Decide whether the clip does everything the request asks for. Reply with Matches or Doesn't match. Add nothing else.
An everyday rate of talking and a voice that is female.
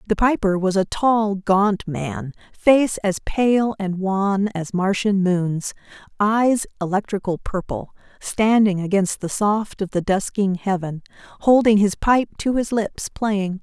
Matches